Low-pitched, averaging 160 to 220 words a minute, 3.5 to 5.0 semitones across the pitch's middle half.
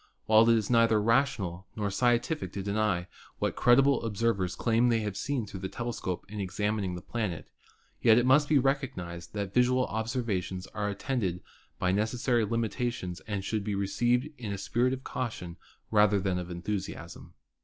Yes: low, 110 Hz; average, 175 wpm; average, 3.9 semitones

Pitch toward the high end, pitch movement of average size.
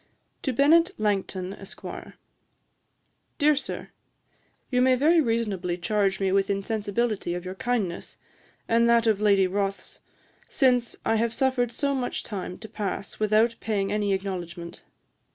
Yes: high, 215 Hz; average, 3.8 semitones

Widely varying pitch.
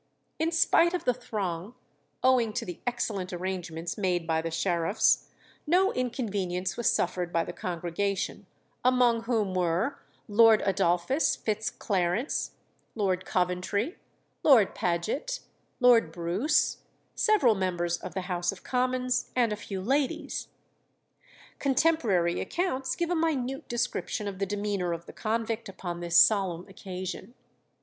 Yes: wide, 5.8 semitones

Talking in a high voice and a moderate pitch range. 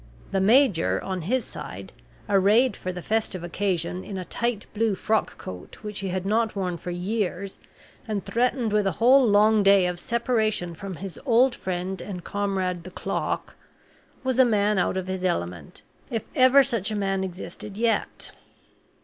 Yes: high, 200 Hz; average, 3.4 semitones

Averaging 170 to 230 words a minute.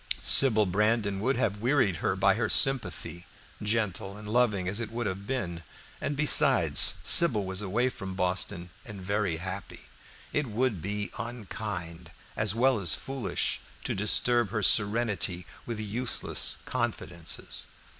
No: average, 140 wpm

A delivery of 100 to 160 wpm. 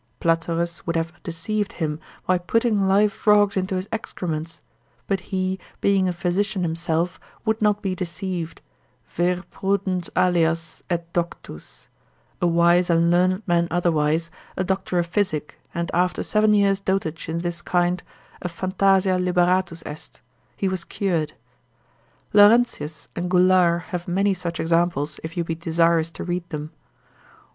Yes: average, 145 wpm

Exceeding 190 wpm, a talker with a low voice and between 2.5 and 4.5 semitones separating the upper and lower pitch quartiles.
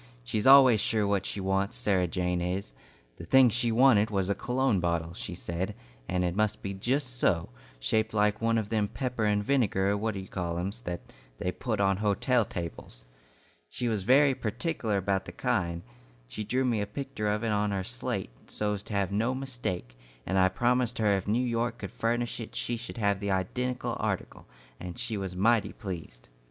Yes: average, 200 wpm; low, 105 Hz; average, 3.9 semitones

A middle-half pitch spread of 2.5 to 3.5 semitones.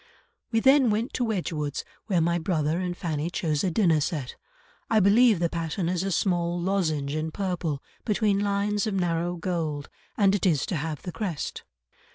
No: average, 3.9 semitones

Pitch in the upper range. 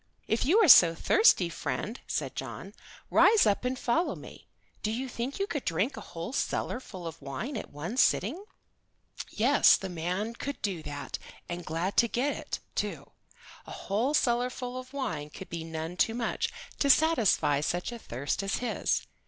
Yes: high, 220 Hz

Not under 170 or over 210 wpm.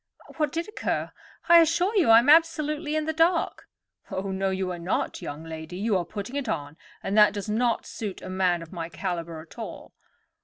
Yes: fast, 205 wpm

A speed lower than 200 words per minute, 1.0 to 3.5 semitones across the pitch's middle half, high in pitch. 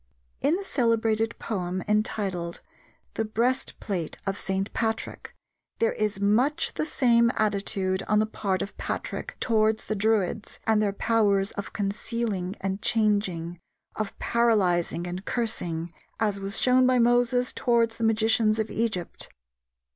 Yes: slow, 135 wpm; average, 2.9 semitones; high, 215 Hz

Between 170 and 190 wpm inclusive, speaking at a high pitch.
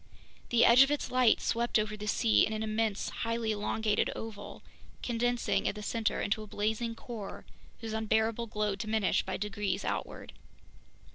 No: average, 160 wpm; high, 220 Hz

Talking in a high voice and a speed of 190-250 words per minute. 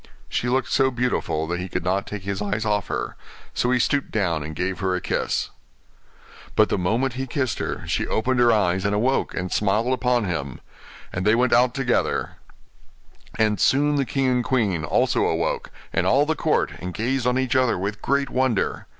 No: low, 115 Hz; average, 200 wpm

